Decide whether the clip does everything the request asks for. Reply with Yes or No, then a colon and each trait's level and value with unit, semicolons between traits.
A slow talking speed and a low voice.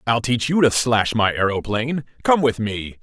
No: average, 200 wpm; low, 120 Hz